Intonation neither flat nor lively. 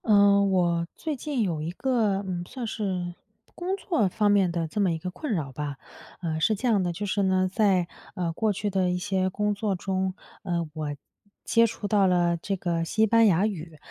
Yes: average, 3.3 semitones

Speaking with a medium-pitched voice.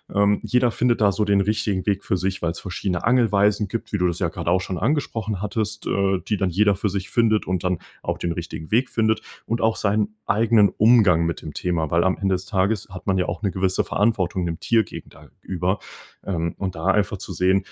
No: low, 100 Hz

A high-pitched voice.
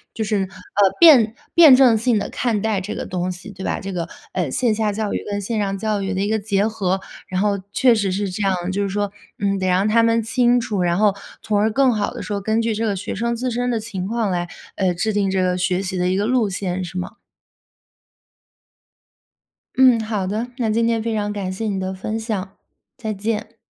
Yes: high, 205 Hz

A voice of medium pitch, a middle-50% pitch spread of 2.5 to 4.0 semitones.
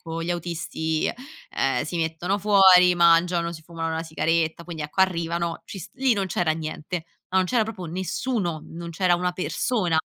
No: medium, 170 Hz; narrow, 2.1 semitones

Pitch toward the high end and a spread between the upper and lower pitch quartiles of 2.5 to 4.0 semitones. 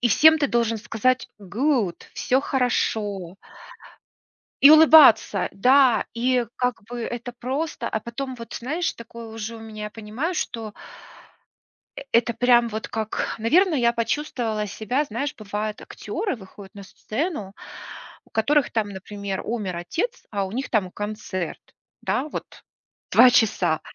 Yes: high, 230 Hz; average, 3.7 semitones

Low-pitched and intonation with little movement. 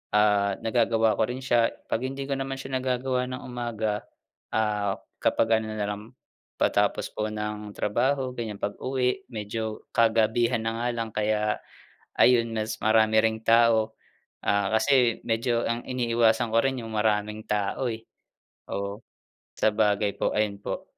Yes: low, 110 Hz; narrow, 2.2 semitones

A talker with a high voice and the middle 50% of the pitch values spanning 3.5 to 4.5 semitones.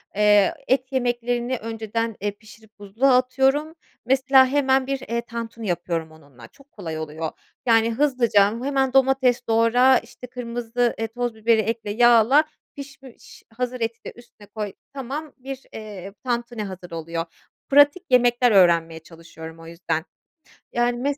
Yes: high, 235 Hz; average, 4.1 semitones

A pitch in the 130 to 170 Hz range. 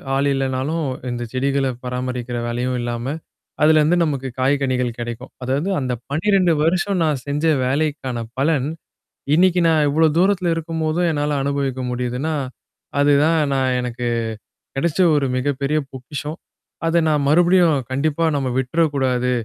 Yes: medium, 140 Hz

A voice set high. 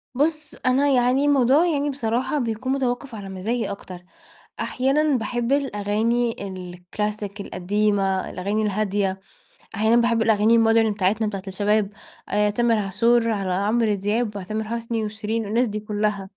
Yes: high, 220 Hz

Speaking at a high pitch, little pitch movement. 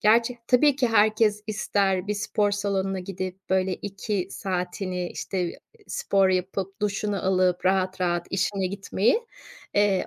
Yes: high, 195 Hz; narrow, 2.0 semitones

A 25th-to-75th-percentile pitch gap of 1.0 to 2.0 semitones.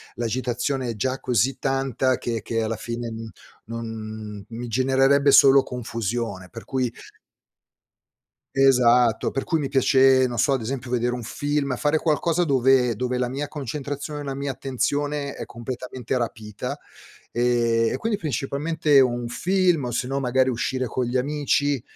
No: average, 2.8 semitones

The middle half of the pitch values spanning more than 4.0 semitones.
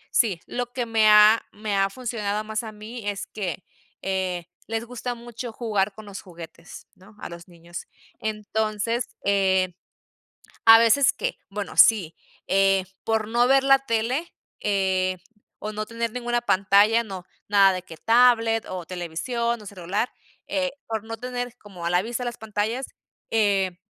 No: average, 3.3 semitones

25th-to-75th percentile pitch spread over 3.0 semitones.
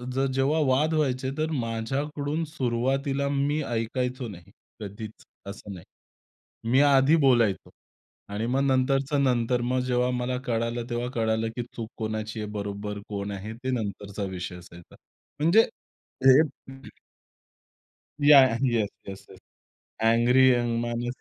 Yes: average, 3.6 semitones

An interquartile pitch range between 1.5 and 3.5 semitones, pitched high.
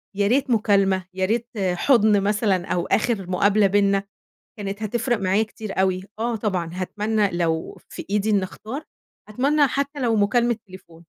Yes: average, 3.2 semitones; high, 205 Hz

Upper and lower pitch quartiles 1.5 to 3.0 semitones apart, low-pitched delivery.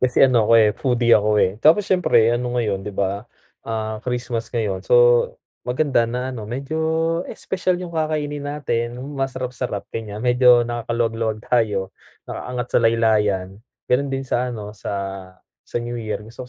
Yes: average, 2.7 semitones; low, 120 Hz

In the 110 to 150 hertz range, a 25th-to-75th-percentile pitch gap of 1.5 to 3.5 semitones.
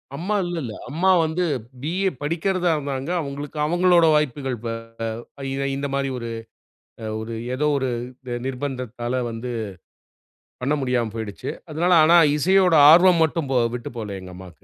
No: medium, 140 Hz; wide, 5.6 semitones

